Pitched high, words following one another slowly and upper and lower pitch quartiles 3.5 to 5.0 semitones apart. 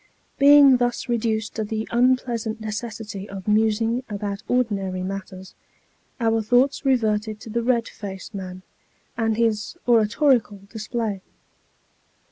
No: high, 220 Hz; slow, 115 wpm; narrow, 2.5 semitones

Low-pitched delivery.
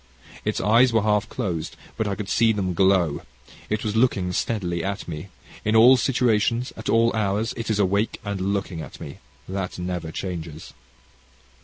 Yes: low, 100 Hz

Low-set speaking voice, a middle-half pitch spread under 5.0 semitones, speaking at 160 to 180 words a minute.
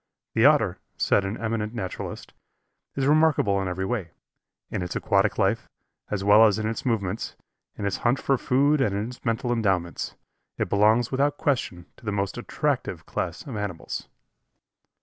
Yes: low, 110 Hz; average, 3.9 semitones; average, 170 wpm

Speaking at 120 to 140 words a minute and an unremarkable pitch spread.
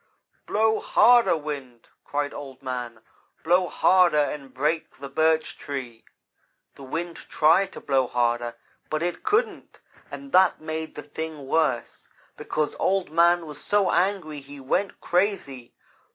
Yes: slow, 135 wpm; average, 4.6 semitones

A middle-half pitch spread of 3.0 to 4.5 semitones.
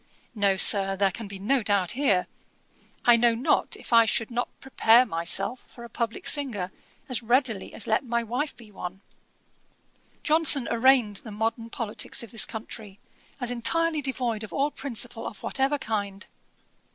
Yes: average, 3.7 semitones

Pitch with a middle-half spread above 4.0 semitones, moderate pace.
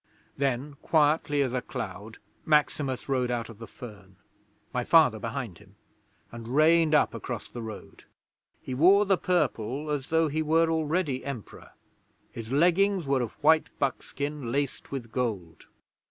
Yes: average, 4.7 semitones; average, 150 wpm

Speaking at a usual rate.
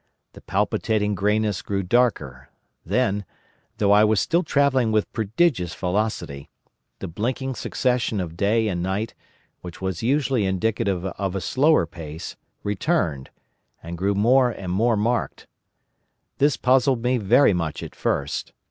No: slow, 130 wpm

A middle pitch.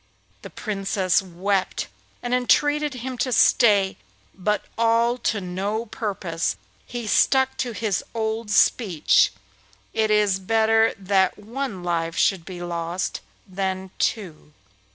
No: high, 205 Hz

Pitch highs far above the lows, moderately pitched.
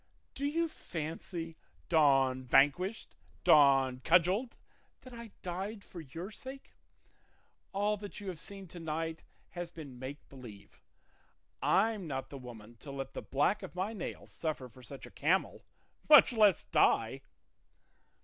Yes: wide, 6.7 semitones; medium, 165 Hz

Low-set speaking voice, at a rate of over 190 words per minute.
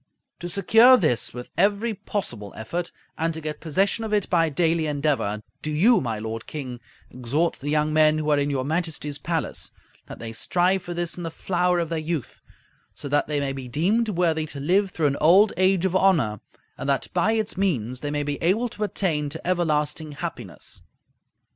No: medium, 160 Hz; average, 200 wpm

